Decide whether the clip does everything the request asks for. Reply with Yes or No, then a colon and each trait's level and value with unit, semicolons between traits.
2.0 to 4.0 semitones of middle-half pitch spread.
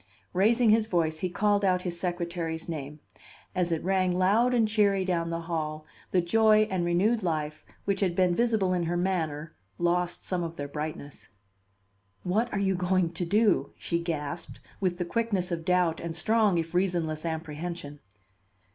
Yes: average, 2.8 semitones